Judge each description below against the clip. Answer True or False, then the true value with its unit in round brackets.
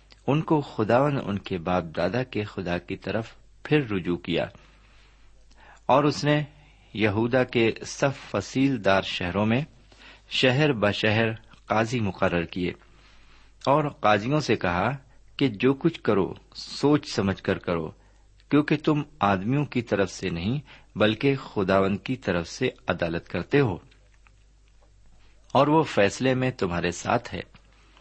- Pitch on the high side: False (110 Hz)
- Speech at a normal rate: True (135 wpm)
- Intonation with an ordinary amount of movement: False (6.0 semitones)